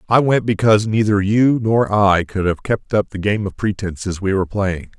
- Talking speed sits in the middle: No, fast, 215 wpm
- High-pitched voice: No, low, 105 Hz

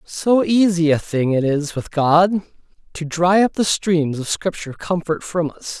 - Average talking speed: Yes, average, 185 wpm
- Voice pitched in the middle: Yes, medium, 170 Hz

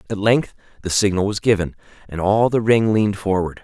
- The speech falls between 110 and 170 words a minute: No, average, 200 wpm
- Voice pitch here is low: Yes, low, 100 Hz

